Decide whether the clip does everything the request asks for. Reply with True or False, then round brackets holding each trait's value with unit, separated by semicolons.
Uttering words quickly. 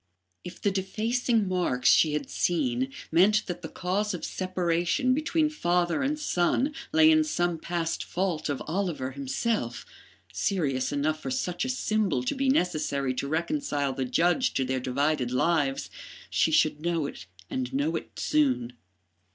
False (155 wpm)